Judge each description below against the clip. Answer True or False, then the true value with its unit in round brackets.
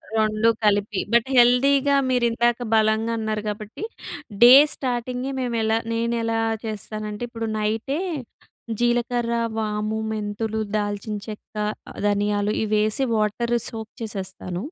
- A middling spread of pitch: False (2.1 semitones)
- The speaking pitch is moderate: False (220 Hz)